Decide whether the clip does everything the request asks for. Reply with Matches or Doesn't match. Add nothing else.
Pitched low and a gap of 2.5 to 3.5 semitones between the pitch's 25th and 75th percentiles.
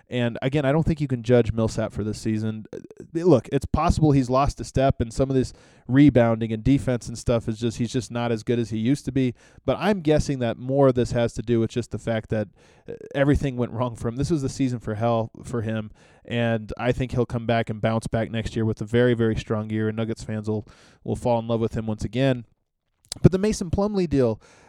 Matches